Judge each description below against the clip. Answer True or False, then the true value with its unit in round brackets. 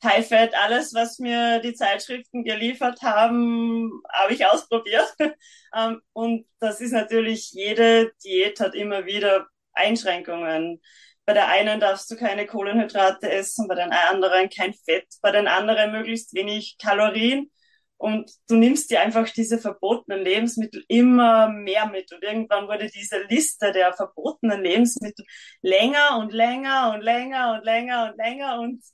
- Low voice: False (220 Hz)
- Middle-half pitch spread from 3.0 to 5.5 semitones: False (2.5 semitones)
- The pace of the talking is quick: False (145 wpm)